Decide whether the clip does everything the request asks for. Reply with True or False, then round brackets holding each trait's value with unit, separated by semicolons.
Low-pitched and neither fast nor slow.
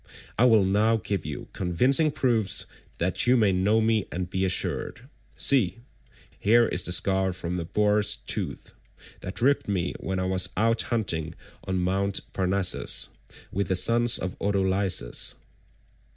True (100 Hz; 150 wpm)